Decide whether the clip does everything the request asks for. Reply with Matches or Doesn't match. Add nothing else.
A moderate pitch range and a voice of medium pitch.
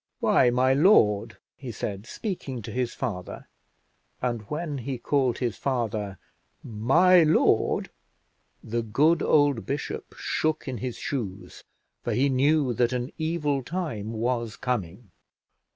Doesn't match